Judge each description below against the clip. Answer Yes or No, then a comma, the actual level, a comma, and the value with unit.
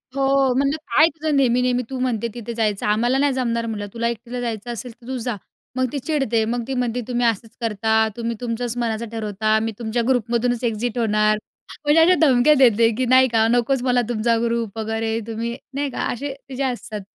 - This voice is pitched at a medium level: No, high, 235 Hz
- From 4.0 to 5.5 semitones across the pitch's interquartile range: No, narrow, 2.4 semitones